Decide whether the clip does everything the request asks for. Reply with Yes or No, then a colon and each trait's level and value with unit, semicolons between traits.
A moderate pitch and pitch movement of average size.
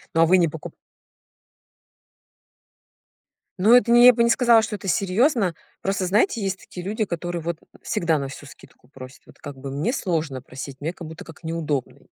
No: medium, 175 Hz; wide, 5.7 semitones